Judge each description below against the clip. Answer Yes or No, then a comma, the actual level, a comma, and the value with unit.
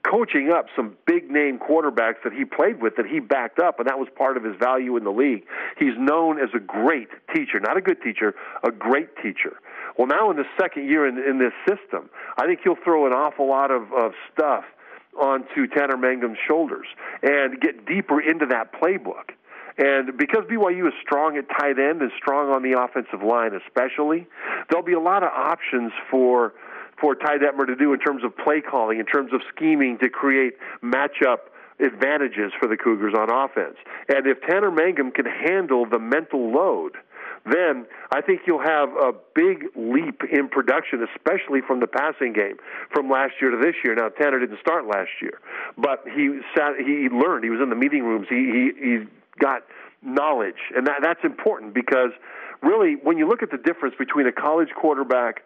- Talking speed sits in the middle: Yes, average, 195 wpm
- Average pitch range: No, wide, 7.0 semitones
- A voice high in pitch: No, medium, 145 Hz